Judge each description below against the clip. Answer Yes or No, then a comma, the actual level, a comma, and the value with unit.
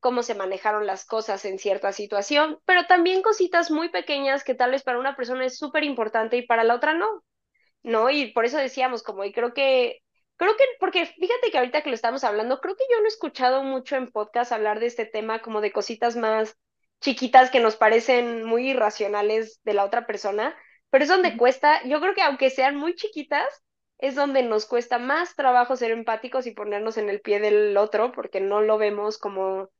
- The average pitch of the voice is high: Yes, high, 245 Hz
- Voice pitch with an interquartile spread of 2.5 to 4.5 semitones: No, average, 4.9 semitones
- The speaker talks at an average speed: No, fast, 210 wpm